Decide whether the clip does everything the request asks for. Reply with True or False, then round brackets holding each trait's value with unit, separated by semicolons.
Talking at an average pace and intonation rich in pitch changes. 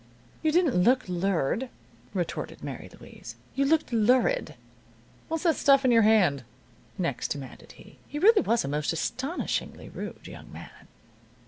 True (145 wpm; 8.7 semitones)